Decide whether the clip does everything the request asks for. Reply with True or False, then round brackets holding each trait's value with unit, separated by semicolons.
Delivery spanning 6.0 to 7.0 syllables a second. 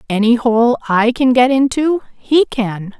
False (3.9 syllables/s)